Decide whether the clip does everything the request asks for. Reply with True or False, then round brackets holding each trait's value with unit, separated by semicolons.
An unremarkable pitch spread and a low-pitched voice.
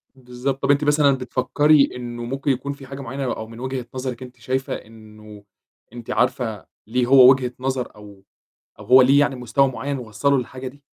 False (2.3 semitones; 130 Hz)